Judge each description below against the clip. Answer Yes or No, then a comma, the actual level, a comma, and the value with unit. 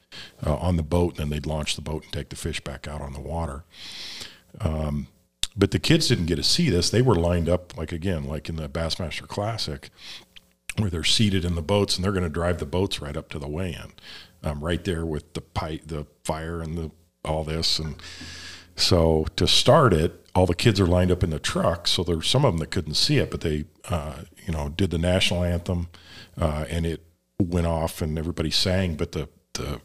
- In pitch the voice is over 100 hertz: No, very low, 85 Hz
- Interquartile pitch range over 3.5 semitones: No, average, 2.8 semitones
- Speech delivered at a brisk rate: Yes, fast, 225 wpm